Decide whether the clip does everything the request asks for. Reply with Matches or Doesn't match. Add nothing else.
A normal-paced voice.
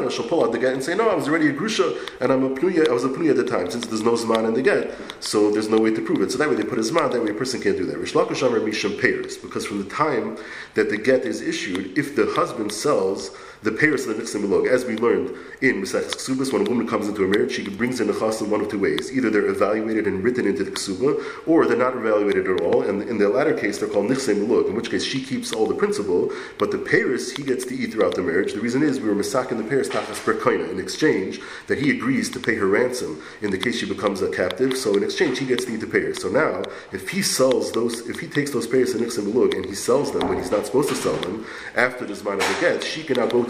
Doesn't match